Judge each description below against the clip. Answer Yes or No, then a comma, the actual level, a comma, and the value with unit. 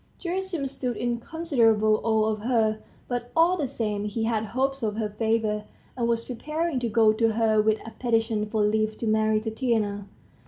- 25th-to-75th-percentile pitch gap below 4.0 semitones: Yes, narrow, 2.4 semitones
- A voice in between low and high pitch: No, high, 225 Hz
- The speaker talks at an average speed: Yes, average, 185 wpm